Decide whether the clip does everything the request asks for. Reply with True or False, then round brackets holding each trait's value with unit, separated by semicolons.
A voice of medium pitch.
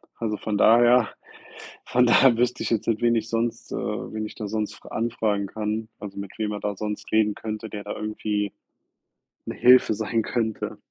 False (110 Hz)